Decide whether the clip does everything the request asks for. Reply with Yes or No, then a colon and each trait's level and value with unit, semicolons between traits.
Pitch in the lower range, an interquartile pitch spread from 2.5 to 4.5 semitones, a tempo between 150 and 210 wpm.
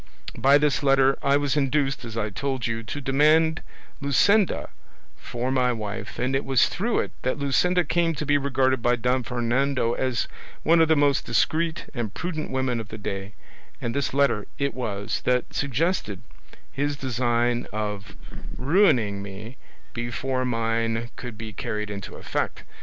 Yes: low, 130 Hz; average, 3.7 semitones; average, 160 wpm